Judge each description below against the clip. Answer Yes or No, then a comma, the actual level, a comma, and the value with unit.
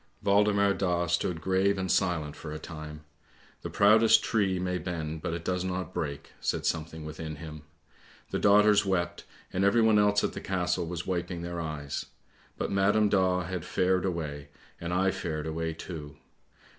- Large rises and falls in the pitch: No, average, 3.3 semitones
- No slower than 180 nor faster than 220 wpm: No, average, 170 wpm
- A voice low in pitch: Yes, very low, 90 Hz